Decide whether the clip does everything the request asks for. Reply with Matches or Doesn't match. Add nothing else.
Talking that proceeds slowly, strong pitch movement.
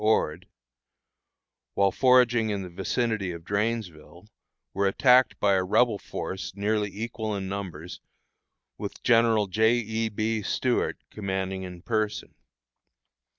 Doesn't match